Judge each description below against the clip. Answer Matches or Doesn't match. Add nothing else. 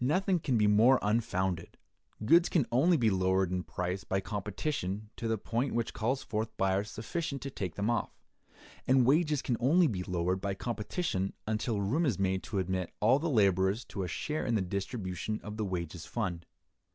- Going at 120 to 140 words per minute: Doesn't match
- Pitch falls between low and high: Doesn't match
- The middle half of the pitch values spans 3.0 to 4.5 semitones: Doesn't match